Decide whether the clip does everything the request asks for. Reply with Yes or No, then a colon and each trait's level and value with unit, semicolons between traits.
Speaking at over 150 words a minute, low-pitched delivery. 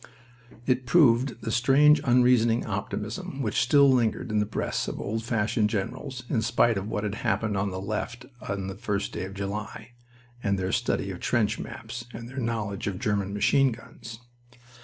Yes: average, 180 wpm; low, 115 Hz